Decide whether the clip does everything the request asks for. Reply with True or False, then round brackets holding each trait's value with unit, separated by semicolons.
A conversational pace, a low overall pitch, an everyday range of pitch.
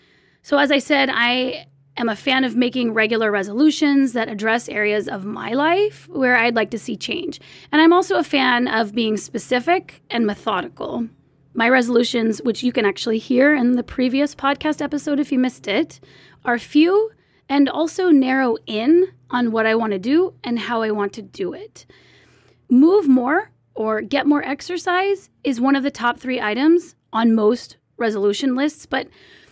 False (175 wpm; 255 Hz; 4.5 semitones)